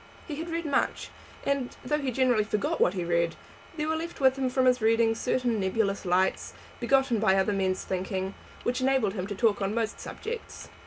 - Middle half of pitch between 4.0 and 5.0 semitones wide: No, wide, 5.5 semitones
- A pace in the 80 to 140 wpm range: No, average, 200 wpm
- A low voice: No, high, 225 Hz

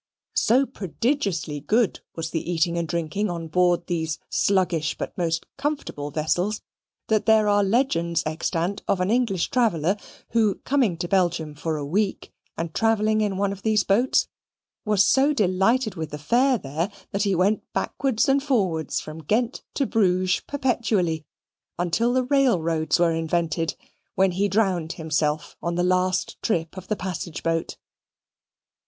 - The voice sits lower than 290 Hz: Yes, medium, 185 Hz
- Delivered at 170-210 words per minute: No, average, 155 wpm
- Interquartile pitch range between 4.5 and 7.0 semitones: Yes, average, 4.8 semitones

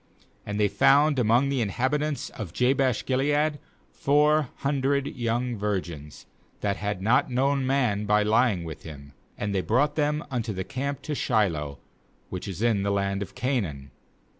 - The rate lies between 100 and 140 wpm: No, average, 160 wpm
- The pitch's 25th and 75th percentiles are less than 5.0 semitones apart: No, wide, 5.6 semitones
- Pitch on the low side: Yes, low, 120 Hz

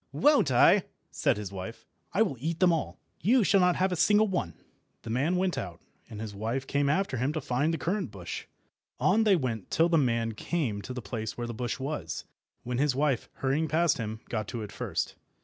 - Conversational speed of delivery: No, fast, 220 wpm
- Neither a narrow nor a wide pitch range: No, wide, 7.2 semitones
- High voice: No, low, 135 Hz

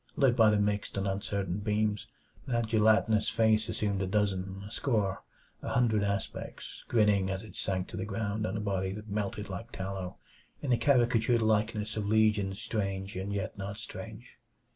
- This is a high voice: No, low, 105 Hz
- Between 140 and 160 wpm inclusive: No, average, 175 wpm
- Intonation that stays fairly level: Yes, narrow, 2.0 semitones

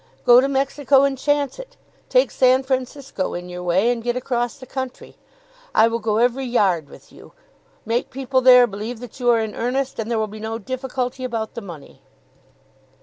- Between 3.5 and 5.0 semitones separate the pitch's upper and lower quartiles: No, average, 3.0 semitones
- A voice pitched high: Yes, high, 245 Hz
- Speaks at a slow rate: No, average, 195 wpm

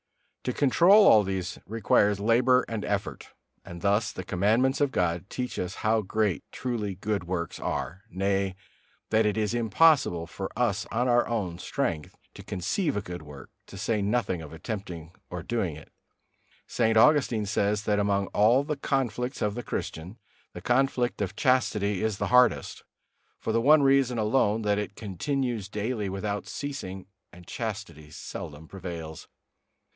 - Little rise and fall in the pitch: No, average, 4.3 semitones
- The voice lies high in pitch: No, low, 105 Hz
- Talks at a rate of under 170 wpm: Yes, average, 160 wpm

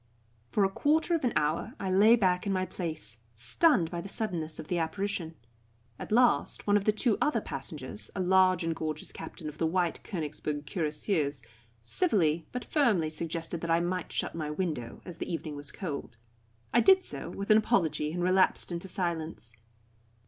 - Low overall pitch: No, medium, 175 Hz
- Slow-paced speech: No, average, 185 wpm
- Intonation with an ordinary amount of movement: Yes, average, 4.4 semitones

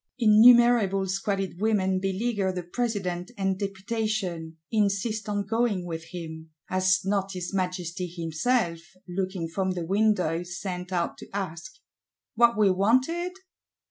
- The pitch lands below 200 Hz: Yes, high, 190 Hz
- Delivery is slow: Yes, slow, 125 wpm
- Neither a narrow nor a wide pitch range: Yes, average, 3.2 semitones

